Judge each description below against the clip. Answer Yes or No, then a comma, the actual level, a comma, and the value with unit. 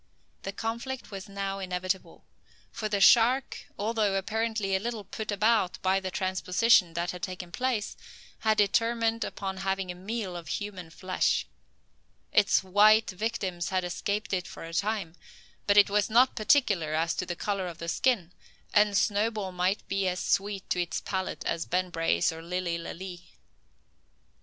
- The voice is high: Yes, high, 195 Hz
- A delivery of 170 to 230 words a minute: No, average, 160 wpm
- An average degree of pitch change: Yes, average, 3.0 semitones